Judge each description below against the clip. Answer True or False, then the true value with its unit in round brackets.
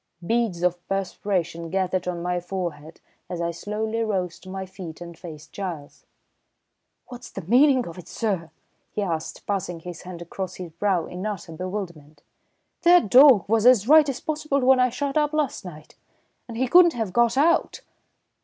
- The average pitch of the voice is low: False (190 Hz)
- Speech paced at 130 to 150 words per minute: False (170 wpm)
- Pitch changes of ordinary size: False (5.7 semitones)